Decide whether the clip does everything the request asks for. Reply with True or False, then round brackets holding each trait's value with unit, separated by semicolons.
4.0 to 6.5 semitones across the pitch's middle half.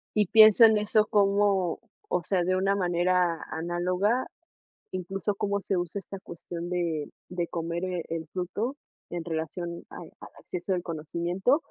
False (2.7 semitones)